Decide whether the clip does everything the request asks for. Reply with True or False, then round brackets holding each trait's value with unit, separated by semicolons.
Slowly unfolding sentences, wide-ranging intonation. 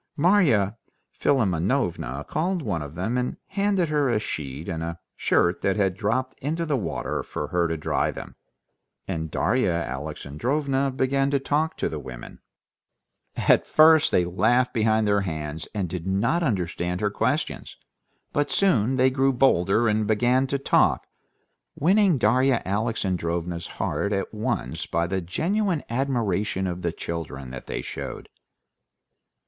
False (145 wpm; 7.8 semitones)